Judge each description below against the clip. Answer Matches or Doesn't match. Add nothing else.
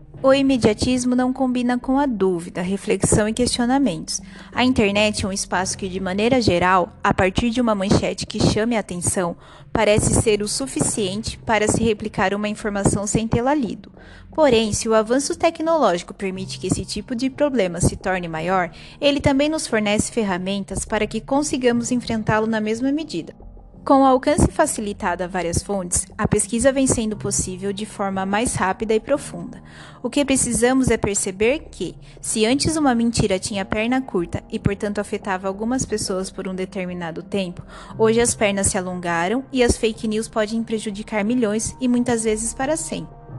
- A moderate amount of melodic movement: Matches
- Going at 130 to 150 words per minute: Doesn't match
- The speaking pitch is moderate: Doesn't match